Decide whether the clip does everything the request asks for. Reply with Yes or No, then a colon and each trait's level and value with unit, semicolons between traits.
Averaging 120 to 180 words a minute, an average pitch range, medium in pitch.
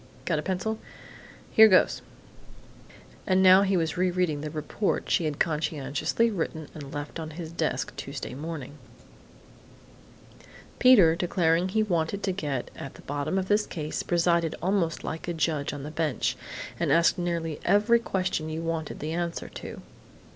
Yes: average, 160 wpm; average, 3.3 semitones; medium, 165 Hz